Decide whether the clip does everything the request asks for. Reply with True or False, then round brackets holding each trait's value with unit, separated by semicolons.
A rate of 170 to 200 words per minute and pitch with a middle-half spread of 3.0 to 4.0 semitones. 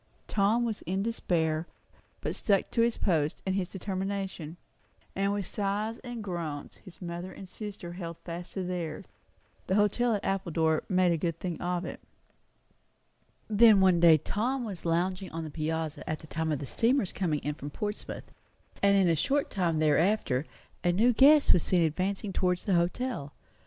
True (175 wpm; 3.7 semitones)